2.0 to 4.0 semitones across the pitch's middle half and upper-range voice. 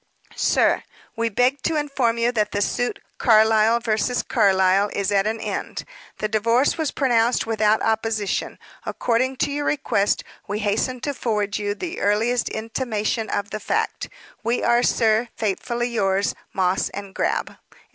Yes: average, 2.8 semitones; high, 225 Hz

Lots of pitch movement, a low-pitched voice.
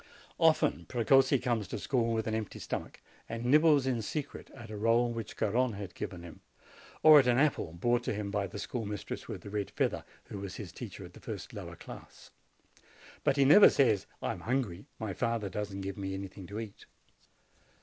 No: average, 4.2 semitones; low, 115 Hz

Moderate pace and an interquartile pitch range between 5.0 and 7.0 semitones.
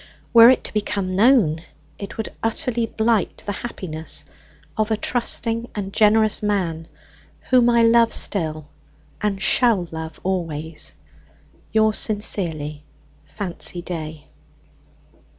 No: slow, 115 wpm; wide, 5.5 semitones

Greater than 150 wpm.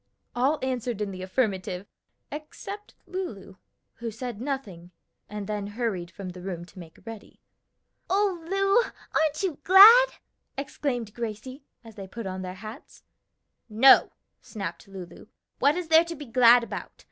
No: average, 145 wpm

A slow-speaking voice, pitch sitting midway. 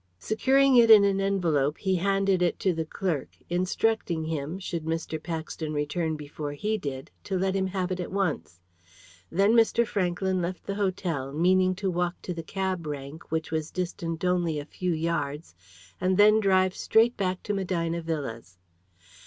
No: average, 170 wpm; medium, 180 Hz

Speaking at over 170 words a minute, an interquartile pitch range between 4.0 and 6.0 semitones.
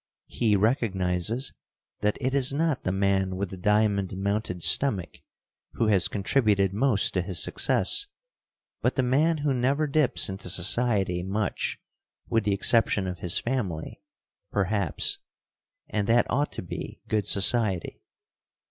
No: average, 140 wpm; average, 4.7 semitones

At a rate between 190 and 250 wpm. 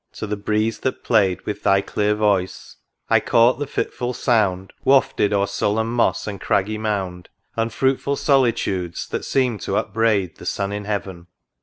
No: average, 160 wpm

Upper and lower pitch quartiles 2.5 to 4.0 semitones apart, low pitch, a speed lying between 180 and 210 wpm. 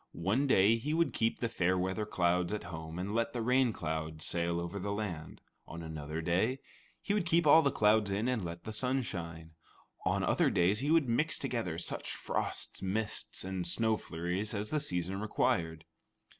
No: average, 5.3 semitones; low, 100 Hz; average, 190 wpm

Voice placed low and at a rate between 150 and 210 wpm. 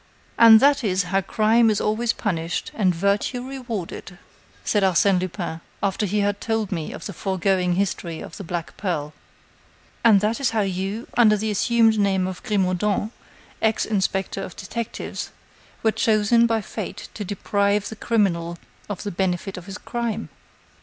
No: high, 200 Hz; average, 160 wpm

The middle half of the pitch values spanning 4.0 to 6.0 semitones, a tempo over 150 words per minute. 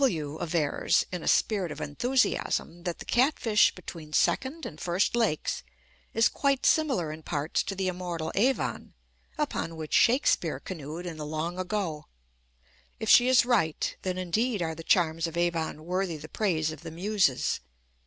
Yes: average, 5.2 semitones; average, 165 wpm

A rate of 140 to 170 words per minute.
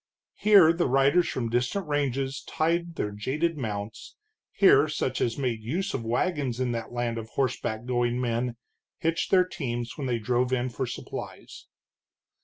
Yes: average, 160 wpm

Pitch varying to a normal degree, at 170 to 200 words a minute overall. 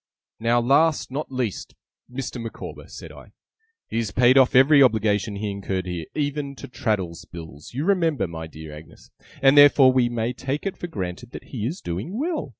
No: wide, 5.8 semitones; average, 185 wpm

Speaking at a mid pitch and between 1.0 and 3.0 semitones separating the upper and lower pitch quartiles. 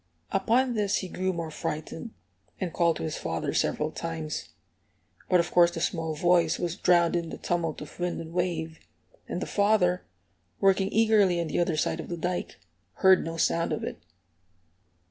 Yes: medium, 175 Hz; narrow, 2.4 semitones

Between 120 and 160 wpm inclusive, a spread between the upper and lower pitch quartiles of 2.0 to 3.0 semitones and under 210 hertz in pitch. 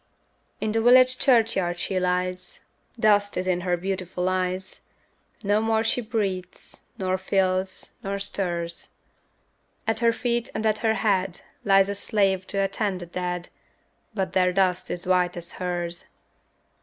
Yes: average, 145 wpm; average, 2.7 semitones; high, 190 Hz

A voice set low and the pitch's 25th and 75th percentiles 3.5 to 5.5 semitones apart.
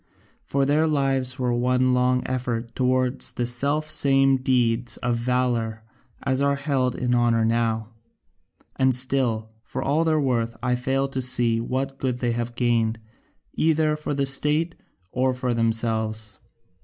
No: low, 125 Hz; narrow, 2.5 semitones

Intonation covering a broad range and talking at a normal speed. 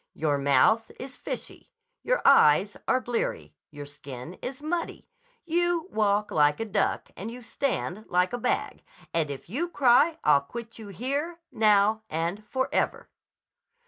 Yes: wide, 8.1 semitones; average, 145 wpm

